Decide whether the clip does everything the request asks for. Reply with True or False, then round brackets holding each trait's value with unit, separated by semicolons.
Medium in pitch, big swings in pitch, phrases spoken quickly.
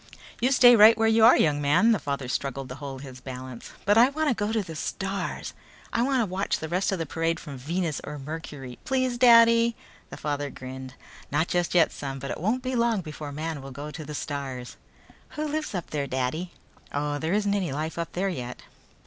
True (165 Hz; 7.7 semitones; 215 wpm)